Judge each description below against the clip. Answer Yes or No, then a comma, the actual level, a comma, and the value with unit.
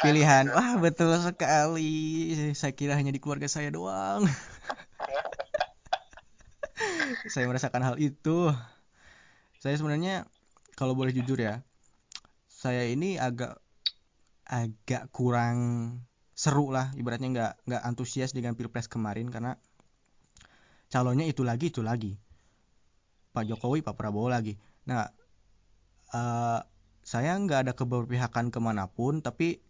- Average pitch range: Yes, average, 4.2 semitones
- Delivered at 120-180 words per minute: No, average, 105 wpm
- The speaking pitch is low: Yes, low, 125 Hz